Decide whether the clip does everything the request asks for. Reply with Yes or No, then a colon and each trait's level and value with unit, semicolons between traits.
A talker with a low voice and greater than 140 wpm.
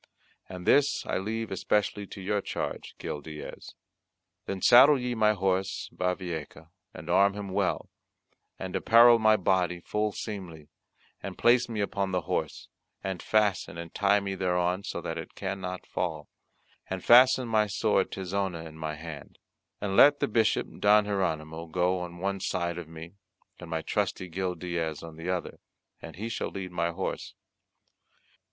Yes: very low, 95 Hz; average, 160 wpm